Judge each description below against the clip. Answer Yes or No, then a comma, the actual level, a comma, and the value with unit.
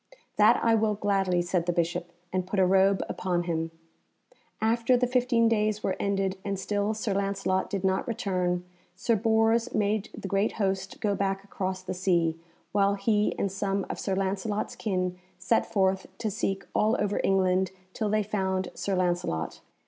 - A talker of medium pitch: No, high, 195 Hz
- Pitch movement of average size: No, narrow, 2.2 semitones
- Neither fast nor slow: Yes, average, 170 wpm